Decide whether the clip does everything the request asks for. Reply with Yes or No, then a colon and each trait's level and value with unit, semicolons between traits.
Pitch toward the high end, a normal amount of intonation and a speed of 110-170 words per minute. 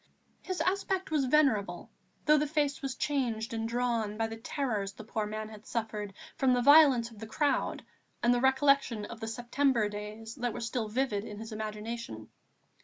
No: high, 230 Hz; average, 3.9 semitones; average, 180 wpm